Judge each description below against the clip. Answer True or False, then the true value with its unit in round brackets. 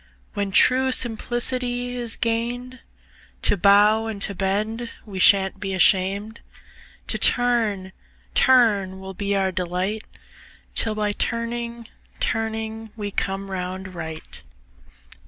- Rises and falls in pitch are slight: False (3.4 semitones)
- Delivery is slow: True (115 wpm)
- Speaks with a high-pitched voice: True (210 Hz)